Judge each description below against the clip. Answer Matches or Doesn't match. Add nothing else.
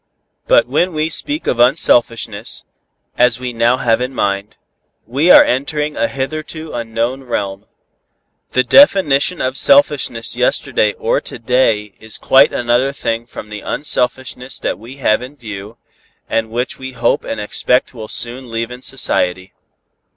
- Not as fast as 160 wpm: Matches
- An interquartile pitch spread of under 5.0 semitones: Matches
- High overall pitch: Doesn't match